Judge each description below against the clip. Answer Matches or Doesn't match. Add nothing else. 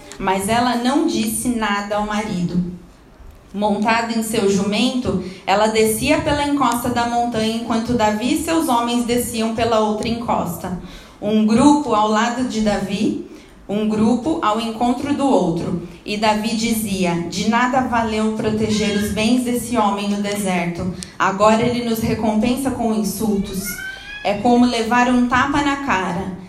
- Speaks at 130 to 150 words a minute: Matches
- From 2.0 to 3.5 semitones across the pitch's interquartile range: Matches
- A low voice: Doesn't match